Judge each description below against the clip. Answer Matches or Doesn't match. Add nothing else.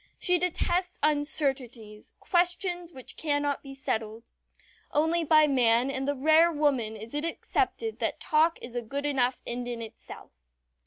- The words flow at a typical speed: Matches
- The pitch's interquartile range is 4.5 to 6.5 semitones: Matches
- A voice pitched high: Matches